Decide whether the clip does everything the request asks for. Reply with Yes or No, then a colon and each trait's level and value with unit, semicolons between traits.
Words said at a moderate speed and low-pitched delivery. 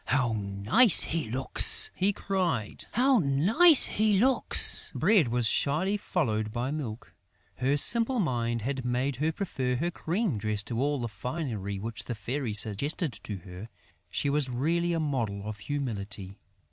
Yes: average, 155 wpm; low, 130 Hz